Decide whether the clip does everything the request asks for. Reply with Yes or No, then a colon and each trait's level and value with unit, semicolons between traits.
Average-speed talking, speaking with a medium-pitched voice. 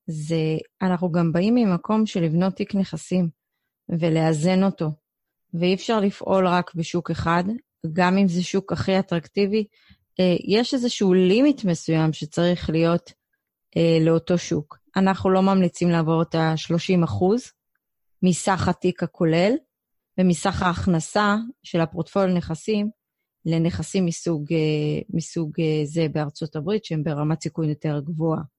Yes: average, 120 wpm; medium, 175 Hz